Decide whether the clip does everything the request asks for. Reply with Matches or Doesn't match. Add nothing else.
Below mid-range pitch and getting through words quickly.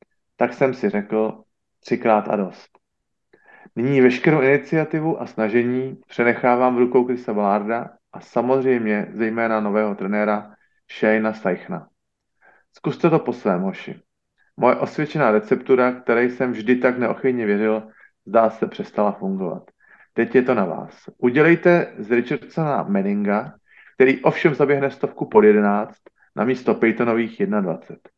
Doesn't match